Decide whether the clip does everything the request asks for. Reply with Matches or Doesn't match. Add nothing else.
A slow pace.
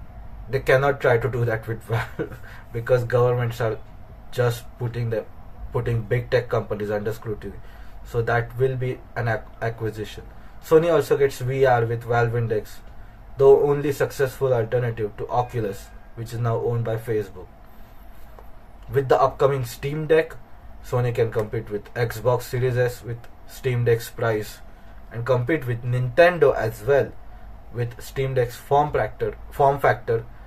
Doesn't match